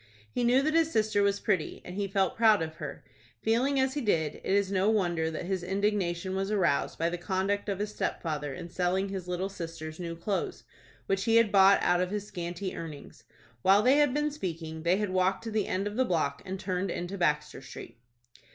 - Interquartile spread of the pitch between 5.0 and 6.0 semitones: No, average, 3.3 semitones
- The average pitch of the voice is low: No, high, 190 Hz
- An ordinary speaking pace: No, fast, 215 wpm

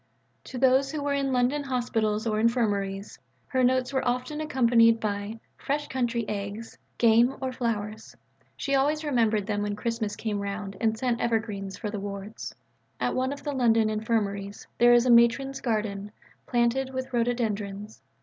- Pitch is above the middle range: Yes, high, 230 Hz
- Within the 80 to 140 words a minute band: No, average, 170 wpm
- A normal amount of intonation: Yes, average, 3.5 semitones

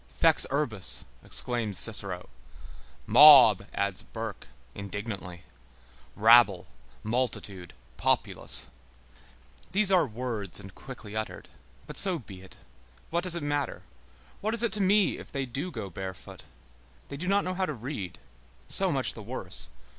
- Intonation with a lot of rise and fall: Yes, wide, 7.3 semitones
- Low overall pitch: Yes, low, 120 Hz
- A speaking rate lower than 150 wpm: Yes, average, 140 wpm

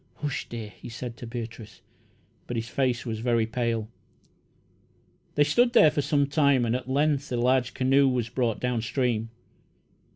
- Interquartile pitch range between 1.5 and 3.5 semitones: Yes, average, 3.1 semitones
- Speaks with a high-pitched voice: No, low, 125 Hz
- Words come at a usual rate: Yes, average, 165 wpm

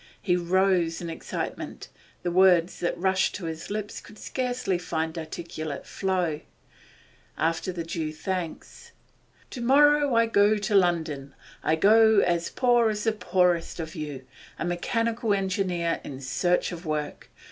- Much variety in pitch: No, average, 4.1 semitones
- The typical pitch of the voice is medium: Yes, medium, 180 Hz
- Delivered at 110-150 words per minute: Yes, average, 145 wpm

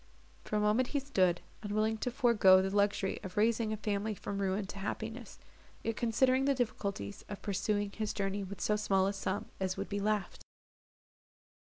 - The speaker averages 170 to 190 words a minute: Yes, average, 180 wpm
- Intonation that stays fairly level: Yes, narrow, 2.2 semitones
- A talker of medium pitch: No, high, 205 Hz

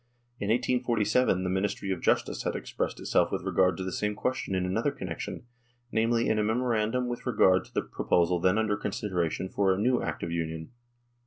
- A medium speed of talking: Yes, average, 195 wpm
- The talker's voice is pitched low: Yes, low, 105 Hz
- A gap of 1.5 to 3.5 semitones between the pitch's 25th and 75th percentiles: No, average, 3.9 semitones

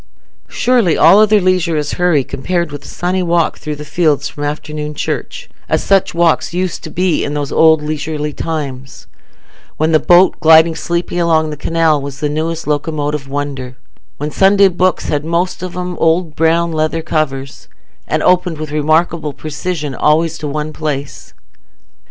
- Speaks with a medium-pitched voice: Yes, medium, 160 Hz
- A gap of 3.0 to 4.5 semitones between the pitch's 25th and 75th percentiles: No, narrow, 2.5 semitones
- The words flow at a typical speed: Yes, average, 165 wpm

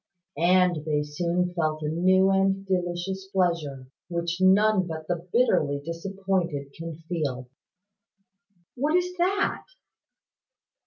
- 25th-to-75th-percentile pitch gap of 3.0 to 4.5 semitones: Yes, average, 3.4 semitones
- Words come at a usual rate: No, slow, 110 wpm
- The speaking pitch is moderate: Yes, medium, 175 Hz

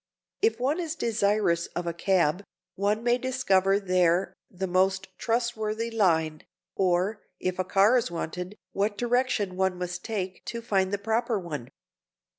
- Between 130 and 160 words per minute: Yes, average, 150 wpm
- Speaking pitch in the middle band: No, high, 195 Hz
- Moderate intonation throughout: Yes, average, 3.9 semitones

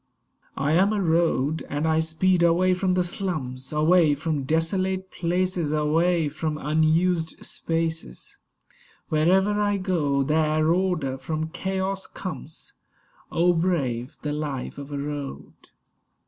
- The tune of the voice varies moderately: Yes, average, 3.4 semitones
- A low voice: No, medium, 160 Hz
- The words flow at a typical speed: No, slow, 125 wpm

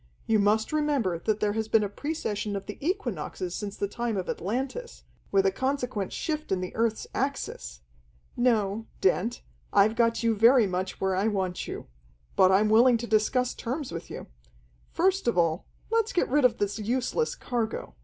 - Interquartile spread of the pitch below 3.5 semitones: No, average, 4.3 semitones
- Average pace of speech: Yes, average, 180 wpm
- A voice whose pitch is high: Yes, high, 220 Hz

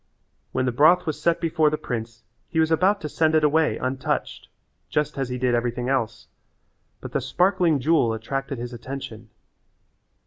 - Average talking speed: Yes, average, 170 wpm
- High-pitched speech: No, low, 135 Hz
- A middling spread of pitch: Yes, average, 4.6 semitones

